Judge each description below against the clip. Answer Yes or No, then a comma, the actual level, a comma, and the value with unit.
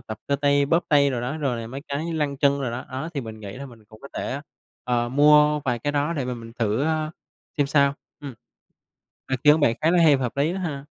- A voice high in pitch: No, medium, 140 Hz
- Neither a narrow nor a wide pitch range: Yes, average, 3.3 semitones